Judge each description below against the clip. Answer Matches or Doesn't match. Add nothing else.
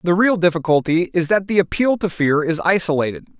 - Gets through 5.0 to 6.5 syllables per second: Matches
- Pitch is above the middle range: Doesn't match